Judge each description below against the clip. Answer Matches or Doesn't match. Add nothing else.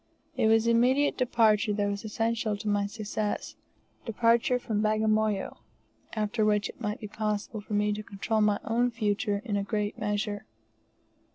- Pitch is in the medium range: Doesn't match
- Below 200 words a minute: Matches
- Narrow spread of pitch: Matches